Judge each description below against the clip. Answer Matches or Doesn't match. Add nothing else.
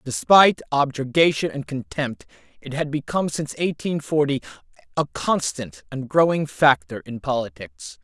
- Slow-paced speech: Matches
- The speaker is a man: Matches